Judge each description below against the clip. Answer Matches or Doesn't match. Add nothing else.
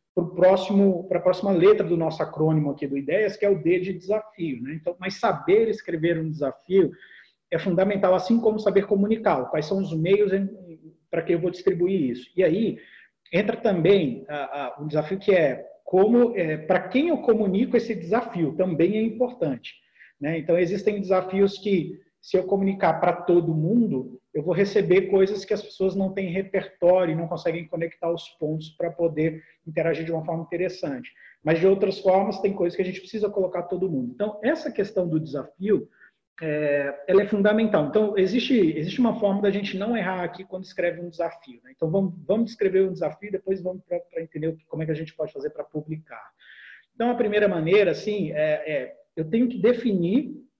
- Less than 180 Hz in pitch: Doesn't match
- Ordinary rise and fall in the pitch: Matches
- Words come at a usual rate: Doesn't match